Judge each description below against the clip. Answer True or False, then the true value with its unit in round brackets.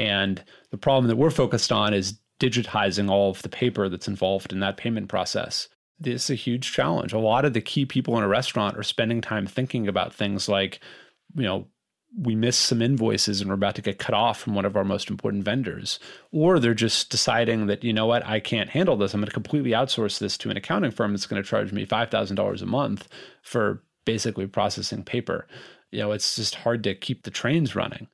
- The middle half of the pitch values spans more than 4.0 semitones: False (3.2 semitones)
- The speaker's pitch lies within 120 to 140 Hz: False (110 Hz)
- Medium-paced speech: False (225 wpm)